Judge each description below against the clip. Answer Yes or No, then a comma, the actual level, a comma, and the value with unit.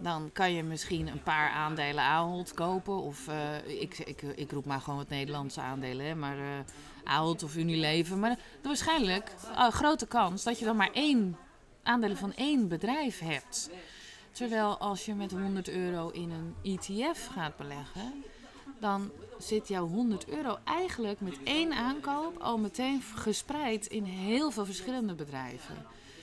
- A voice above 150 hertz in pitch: Yes, high, 190 Hz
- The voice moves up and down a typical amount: No, wide, 7.1 semitones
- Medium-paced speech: Yes, average, 160 wpm